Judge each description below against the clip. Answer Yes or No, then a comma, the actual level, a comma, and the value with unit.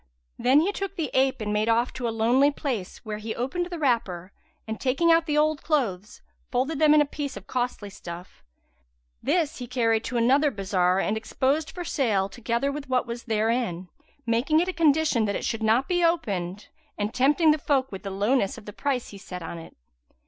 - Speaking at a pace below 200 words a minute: No, fast, 205 wpm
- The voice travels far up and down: Yes, wide, 5.8 semitones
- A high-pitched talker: Yes, high, 245 Hz